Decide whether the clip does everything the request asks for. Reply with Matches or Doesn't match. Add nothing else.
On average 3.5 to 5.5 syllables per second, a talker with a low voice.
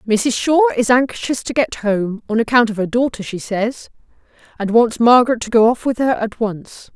Doesn't match